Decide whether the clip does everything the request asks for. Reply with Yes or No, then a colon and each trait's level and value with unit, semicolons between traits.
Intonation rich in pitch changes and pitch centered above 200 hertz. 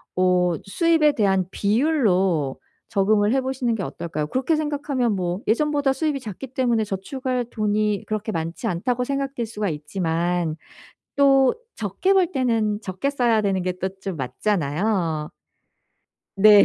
Yes: wide, 6.2 semitones; high, 215 Hz